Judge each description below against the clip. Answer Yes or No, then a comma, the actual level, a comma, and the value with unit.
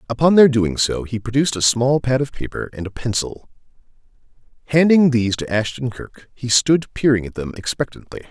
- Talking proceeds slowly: No, average, 180 wpm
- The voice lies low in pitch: Yes, low, 125 Hz